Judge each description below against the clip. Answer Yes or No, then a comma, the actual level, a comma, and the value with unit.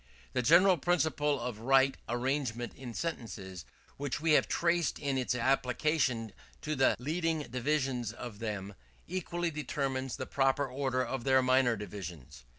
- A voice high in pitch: No, low, 130 Hz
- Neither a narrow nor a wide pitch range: Yes, average, 3.9 semitones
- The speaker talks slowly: No, average, 145 wpm